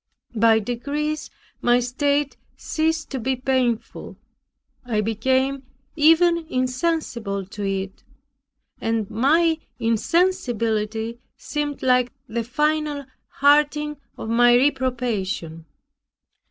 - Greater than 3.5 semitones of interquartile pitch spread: Yes, average, 4.8 semitones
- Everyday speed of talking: No, slow, 90 wpm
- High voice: Yes, very high, 255 Hz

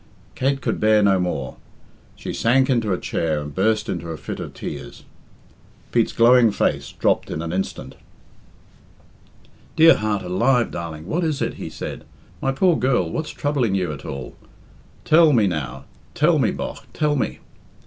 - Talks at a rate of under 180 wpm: Yes, average, 165 wpm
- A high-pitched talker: No, low, 110 Hz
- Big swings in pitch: Yes, wide, 7.9 semitones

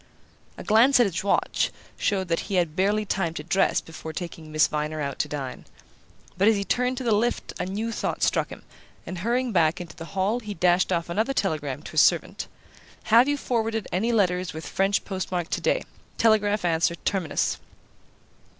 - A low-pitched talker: No, high, 190 Hz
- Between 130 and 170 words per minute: No, average, 185 wpm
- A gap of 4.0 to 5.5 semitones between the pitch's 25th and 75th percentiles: Yes, average, 4.7 semitones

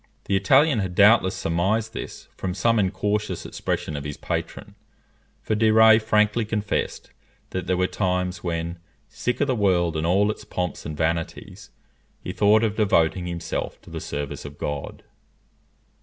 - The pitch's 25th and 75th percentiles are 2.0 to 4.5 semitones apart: Yes, average, 4.0 semitones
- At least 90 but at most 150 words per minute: No, average, 160 wpm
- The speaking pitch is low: Yes, very low, 95 Hz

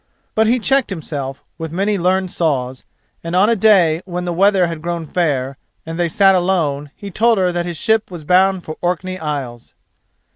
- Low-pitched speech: No, medium, 175 Hz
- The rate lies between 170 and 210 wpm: Yes, average, 190 wpm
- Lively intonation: No, average, 3.6 semitones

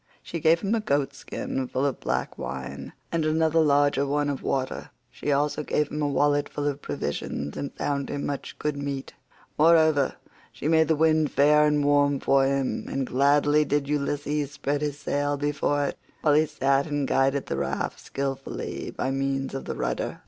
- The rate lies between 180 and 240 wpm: Yes, average, 190 wpm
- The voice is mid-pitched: Yes, medium, 145 Hz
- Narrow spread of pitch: Yes, narrow, 1.4 semitones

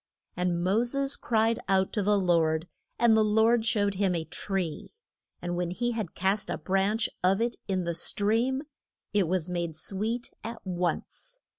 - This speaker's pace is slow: No, average, 170 wpm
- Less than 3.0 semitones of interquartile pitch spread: No, average, 4.1 semitones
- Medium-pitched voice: No, high, 195 Hz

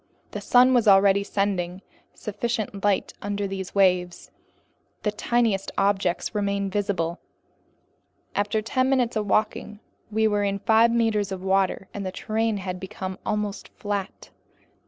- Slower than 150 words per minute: Yes, slow, 135 wpm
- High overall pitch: Yes, high, 205 Hz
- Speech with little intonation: Yes, narrow, 2.0 semitones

